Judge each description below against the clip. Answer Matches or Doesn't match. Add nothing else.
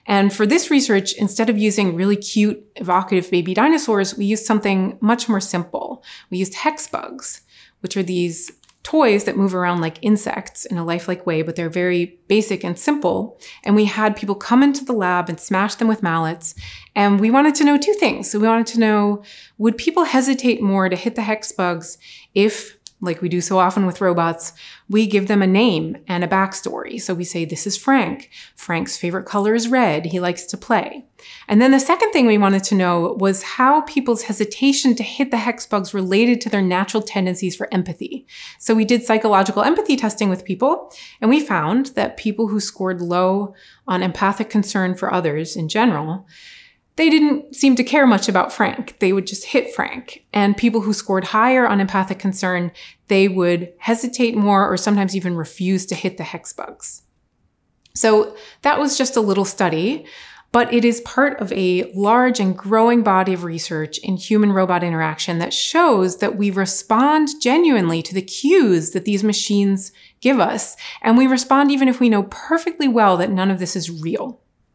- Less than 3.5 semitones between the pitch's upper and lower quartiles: Doesn't match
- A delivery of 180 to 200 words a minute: Matches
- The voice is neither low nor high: Doesn't match